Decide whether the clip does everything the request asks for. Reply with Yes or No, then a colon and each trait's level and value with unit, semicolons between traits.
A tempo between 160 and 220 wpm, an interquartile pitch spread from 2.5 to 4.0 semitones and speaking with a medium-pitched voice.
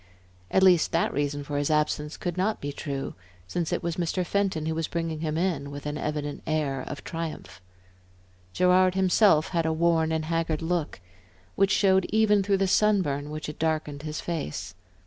Yes: average, 185 wpm; average, 3.5 semitones; medium, 160 Hz